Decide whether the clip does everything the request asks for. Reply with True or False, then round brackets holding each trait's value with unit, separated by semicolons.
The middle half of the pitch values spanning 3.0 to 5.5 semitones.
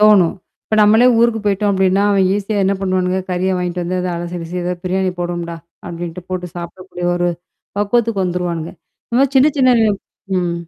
False (2.6 semitones)